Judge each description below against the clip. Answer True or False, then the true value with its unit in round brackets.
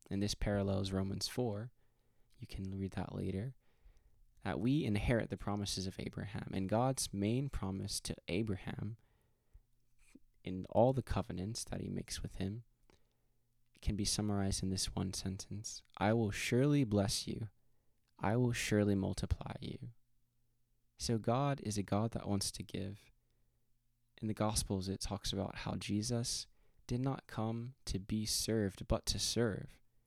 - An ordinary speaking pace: True (150 wpm)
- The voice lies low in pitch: True (110 Hz)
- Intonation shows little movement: False (3.5 semitones)